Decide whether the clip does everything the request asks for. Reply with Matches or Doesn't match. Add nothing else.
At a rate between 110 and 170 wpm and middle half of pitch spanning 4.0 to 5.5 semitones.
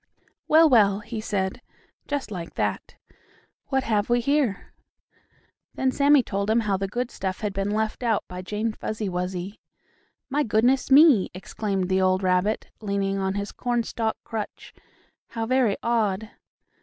Doesn't match